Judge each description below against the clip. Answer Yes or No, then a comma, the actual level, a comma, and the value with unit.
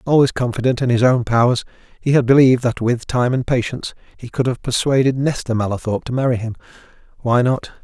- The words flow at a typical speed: Yes, average, 185 wpm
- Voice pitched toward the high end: No, low, 125 Hz